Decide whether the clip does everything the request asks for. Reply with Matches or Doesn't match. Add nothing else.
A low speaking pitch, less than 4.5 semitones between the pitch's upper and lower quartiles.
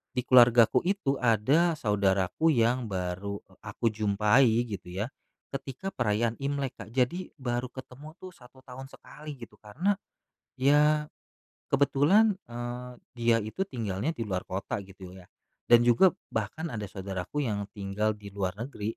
Doesn't match